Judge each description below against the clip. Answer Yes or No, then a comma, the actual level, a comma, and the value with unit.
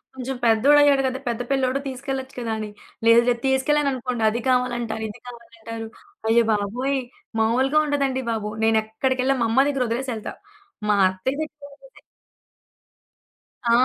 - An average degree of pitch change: Yes, average, 3.0 semitones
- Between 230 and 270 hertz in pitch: Yes, very high, 250 Hz